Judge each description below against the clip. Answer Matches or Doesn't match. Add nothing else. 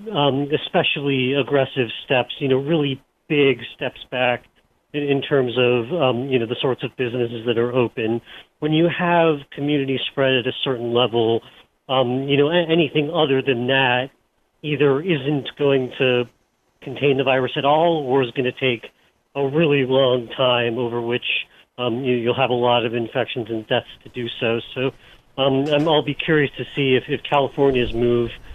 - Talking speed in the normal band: Matches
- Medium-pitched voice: Doesn't match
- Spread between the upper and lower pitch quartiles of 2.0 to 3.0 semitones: Matches